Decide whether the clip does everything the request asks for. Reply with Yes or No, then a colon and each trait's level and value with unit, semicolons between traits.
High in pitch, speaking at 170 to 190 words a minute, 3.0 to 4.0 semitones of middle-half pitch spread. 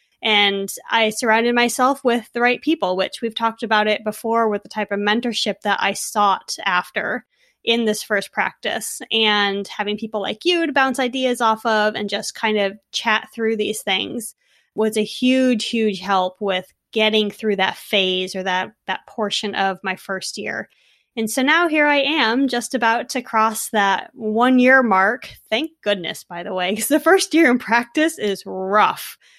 Yes: high, 220 Hz; average, 185 wpm; average, 3.3 semitones